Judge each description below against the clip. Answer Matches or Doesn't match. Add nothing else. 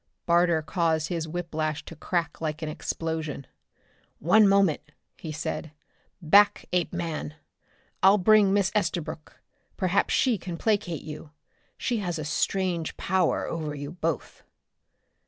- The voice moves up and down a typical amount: Matches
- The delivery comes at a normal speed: Doesn't match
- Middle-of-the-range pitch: Matches